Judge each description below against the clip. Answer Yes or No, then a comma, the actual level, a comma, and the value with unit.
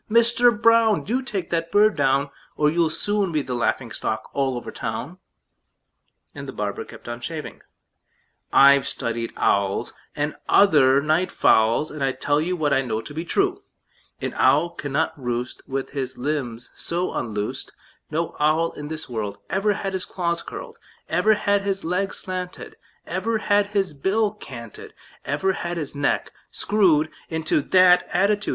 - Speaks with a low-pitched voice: No, medium, 160 Hz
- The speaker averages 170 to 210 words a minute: No, average, 160 wpm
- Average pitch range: No, wide, 6.3 semitones